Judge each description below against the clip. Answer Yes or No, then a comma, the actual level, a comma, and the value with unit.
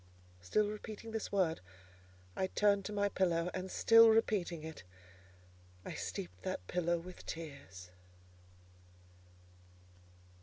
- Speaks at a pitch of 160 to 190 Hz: Yes, medium, 185 Hz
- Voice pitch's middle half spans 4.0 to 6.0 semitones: Yes, average, 4.3 semitones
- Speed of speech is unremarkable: No, slow, 110 wpm